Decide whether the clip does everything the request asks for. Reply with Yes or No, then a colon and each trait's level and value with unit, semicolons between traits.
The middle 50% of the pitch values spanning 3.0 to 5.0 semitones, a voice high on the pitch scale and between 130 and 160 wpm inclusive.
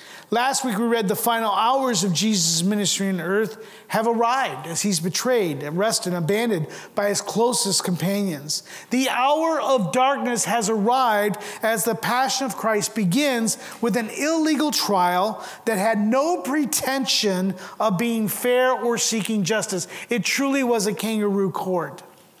Yes: average, 4.1 semitones; high, 220 Hz; average, 150 wpm